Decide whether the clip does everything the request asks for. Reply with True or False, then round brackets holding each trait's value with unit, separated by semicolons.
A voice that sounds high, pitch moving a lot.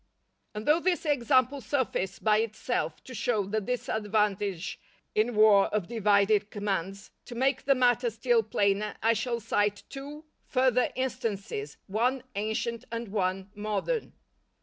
False (220 Hz; 3.6 semitones)